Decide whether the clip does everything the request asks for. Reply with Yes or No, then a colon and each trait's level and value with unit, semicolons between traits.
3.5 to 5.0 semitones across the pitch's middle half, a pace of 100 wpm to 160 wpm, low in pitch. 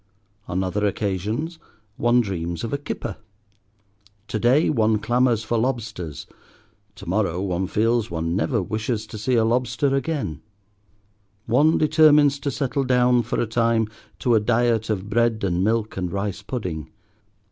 Yes: average, 3.8 semitones; average, 150 wpm; low, 115 Hz